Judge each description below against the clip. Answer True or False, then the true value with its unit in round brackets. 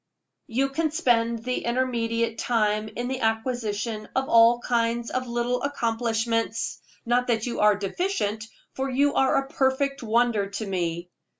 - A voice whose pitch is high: True (235 Hz)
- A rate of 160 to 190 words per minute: False (145 wpm)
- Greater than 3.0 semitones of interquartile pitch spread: False (2.4 semitones)